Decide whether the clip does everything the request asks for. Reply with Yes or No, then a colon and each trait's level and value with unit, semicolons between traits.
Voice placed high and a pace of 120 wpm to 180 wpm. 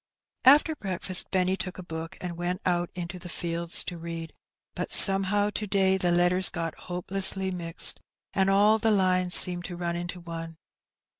No: medium, 180 Hz; average, 170 wpm